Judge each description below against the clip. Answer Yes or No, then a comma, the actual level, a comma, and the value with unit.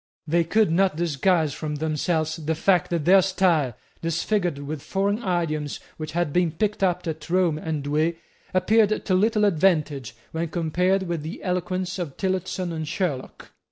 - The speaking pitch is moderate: Yes, medium, 170 Hz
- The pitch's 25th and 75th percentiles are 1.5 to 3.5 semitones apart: Yes, average, 3.2 semitones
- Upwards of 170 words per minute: No, average, 160 wpm